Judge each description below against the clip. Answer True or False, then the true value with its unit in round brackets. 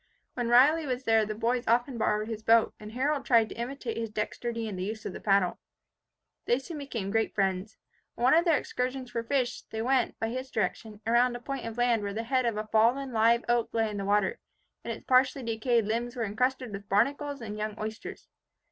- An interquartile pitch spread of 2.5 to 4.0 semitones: True (2.8 semitones)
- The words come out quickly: True (220 wpm)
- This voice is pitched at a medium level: False (230 Hz)